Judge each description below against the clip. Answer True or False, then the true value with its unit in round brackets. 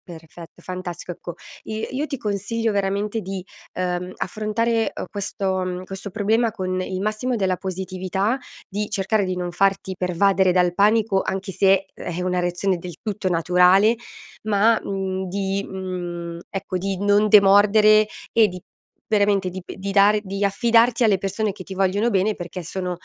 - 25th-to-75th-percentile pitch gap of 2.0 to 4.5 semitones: True (2.4 semitones)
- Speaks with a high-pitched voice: True (195 Hz)